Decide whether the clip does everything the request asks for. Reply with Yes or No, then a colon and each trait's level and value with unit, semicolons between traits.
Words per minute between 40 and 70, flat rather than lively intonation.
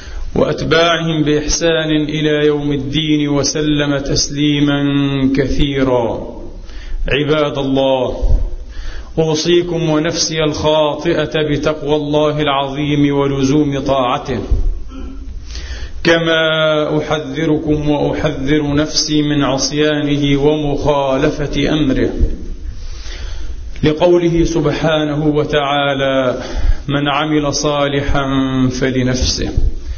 Yes: slow, 65 wpm; narrow, 2.3 semitones